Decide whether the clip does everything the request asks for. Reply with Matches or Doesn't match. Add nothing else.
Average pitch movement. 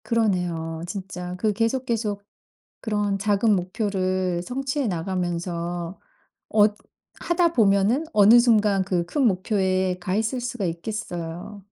Matches